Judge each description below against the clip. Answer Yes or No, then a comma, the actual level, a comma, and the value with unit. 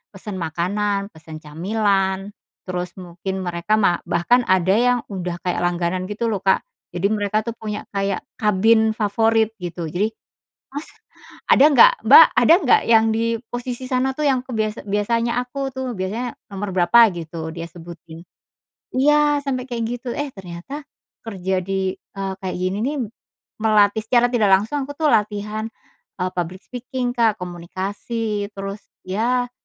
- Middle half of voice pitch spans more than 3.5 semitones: Yes, average, 4.5 semitones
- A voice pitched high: Yes, high, 205 Hz